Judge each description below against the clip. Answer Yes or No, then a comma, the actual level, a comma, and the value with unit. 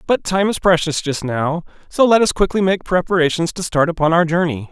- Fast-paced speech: Yes, fast, 215 wpm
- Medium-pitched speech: Yes, medium, 170 Hz